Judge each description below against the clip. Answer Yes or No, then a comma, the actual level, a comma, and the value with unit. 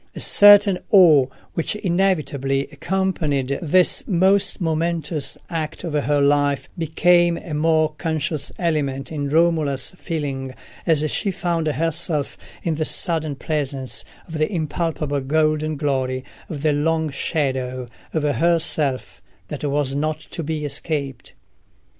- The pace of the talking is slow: Yes, slow, 125 wpm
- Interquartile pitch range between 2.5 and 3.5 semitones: Yes, average, 2.8 semitones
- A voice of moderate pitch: Yes, medium, 155 Hz